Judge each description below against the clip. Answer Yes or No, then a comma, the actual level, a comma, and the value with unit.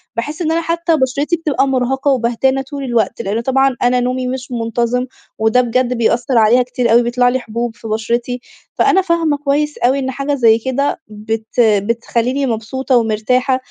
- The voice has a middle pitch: No, very high, 250 Hz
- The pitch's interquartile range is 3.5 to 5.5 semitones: No, average, 2.7 semitones